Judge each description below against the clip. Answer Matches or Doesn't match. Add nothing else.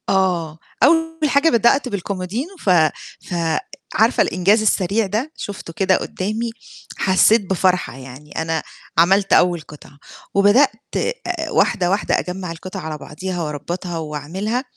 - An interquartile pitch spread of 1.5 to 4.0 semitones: Doesn't match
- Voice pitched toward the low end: Doesn't match